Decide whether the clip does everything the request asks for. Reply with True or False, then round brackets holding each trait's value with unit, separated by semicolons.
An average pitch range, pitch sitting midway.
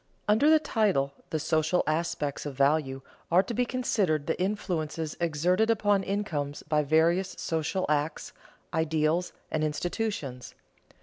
True (4.5 semitones; 160 Hz)